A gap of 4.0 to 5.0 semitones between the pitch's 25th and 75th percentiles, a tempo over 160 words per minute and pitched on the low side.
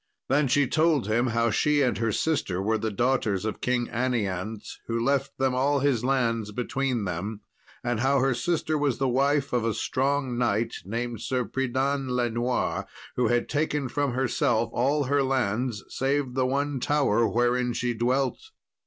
No: average, 2.9 semitones; average, 170 wpm; low, 125 Hz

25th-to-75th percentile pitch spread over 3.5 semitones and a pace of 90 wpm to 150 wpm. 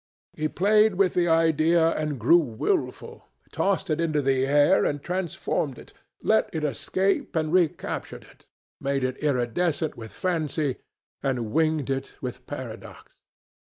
Yes: average, 4.1 semitones; average, 140 wpm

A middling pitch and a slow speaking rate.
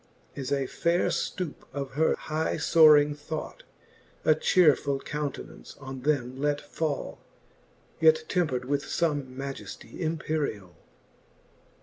Yes: medium, 145 Hz; slow, 110 wpm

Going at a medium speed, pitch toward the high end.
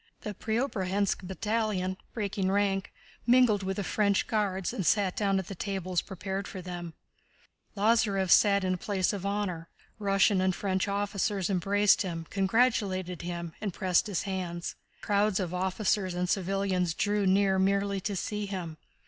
Yes: average, 155 wpm; high, 195 Hz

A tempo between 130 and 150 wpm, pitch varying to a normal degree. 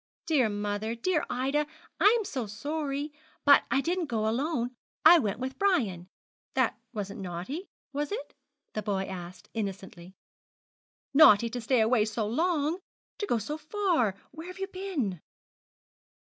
No: average, 145 wpm; wide, 7.1 semitones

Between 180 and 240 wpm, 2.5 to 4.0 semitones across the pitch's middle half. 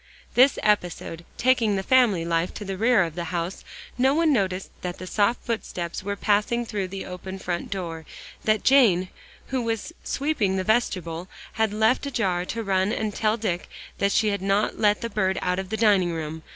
Yes: average, 190 wpm; average, 3.7 semitones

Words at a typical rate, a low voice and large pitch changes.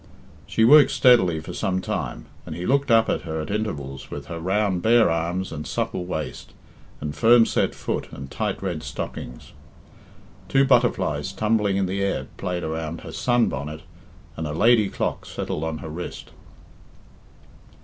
Yes: average, 165 wpm; very low, 90 Hz; wide, 6.0 semitones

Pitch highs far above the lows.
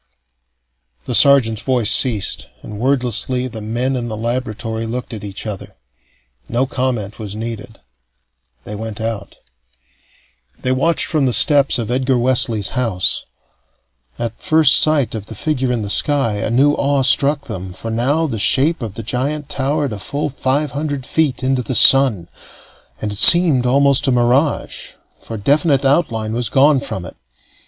No: average, 3.8 semitones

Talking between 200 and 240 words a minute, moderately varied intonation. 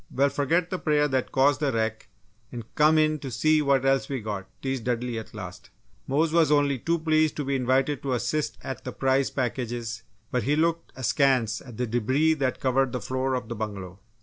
Yes: fast, 205 wpm; average, 3.6 semitones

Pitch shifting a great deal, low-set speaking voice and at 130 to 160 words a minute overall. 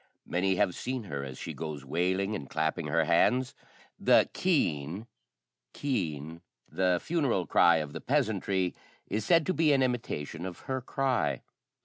Yes: wide, 8.5 semitones; very low, 90 Hz; average, 150 wpm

